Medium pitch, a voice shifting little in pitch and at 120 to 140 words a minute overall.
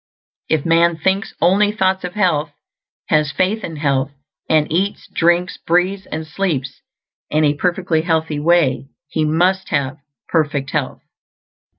No: medium, 165 Hz; average, 3.3 semitones; slow, 135 wpm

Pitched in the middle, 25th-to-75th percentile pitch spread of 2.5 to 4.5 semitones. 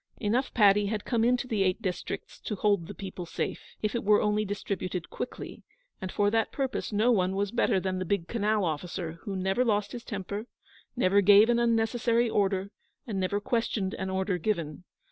No: high, 205 Hz; average, 3.0 semitones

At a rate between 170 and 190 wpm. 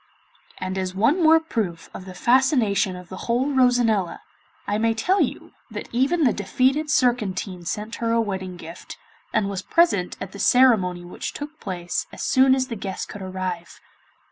Yes: average, 175 wpm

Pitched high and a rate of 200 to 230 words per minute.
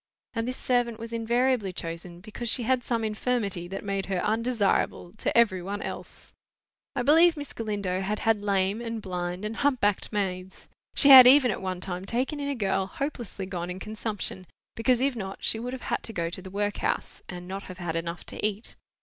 Yes: high, 210 Hz; fast, 205 wpm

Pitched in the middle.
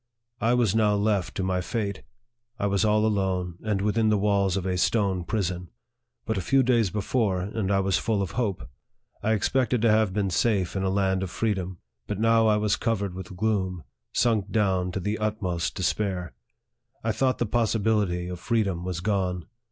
No: low, 100 Hz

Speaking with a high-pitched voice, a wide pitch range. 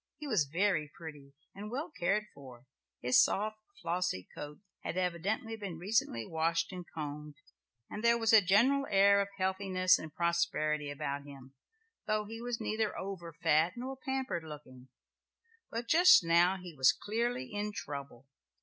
No: medium, 180 Hz; wide, 6.0 semitones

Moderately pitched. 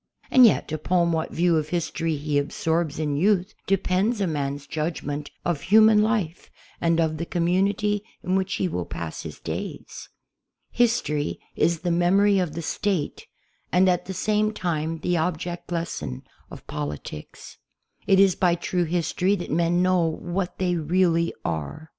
Yes: medium, 175 Hz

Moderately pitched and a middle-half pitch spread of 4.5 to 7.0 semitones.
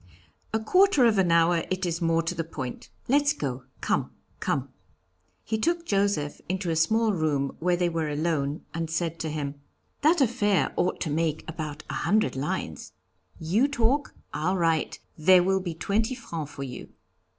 Yes: medium, 170 Hz; average, 5.1 semitones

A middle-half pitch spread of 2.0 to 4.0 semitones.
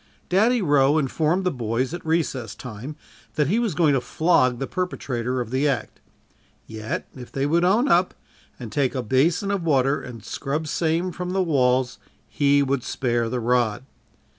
No: average, 5.3 semitones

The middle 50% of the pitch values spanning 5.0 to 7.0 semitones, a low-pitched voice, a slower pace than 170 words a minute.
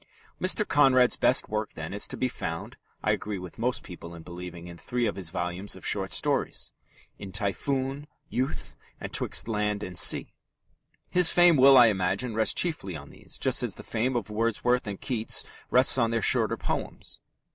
No: wide, 5.6 semitones; low, 110 Hz; average, 185 wpm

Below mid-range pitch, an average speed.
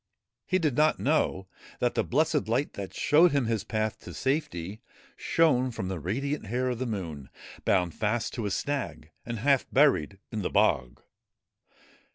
Yes: low, 120 Hz; average, 170 wpm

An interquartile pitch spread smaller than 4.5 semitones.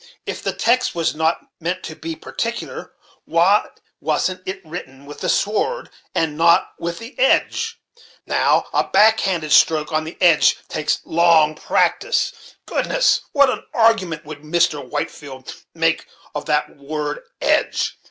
No: average, 5.1 semitones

